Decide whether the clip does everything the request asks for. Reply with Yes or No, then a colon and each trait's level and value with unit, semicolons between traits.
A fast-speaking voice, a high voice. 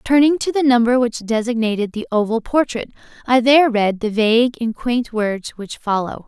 No: average, 180 wpm; high, 235 Hz